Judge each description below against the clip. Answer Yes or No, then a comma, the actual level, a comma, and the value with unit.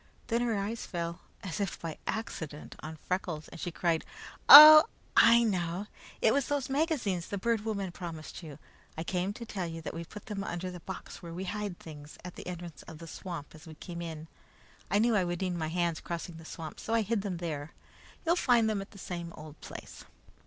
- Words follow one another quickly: Yes, fast, 220 wpm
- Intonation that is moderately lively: Yes, average, 4.2 semitones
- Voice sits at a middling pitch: Yes, medium, 180 Hz